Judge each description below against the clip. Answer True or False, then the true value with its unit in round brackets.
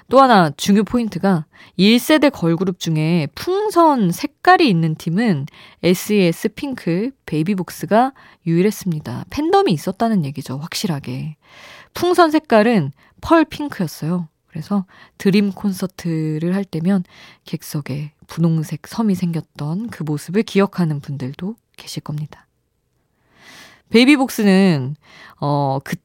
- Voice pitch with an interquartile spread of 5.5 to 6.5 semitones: True (5.8 semitones)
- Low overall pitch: False (185 Hz)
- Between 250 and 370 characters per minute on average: True (265 characters per minute)